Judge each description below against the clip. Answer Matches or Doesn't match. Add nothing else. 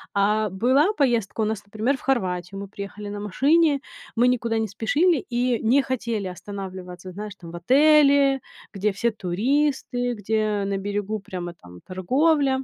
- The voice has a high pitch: Matches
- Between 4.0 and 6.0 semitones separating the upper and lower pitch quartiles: Matches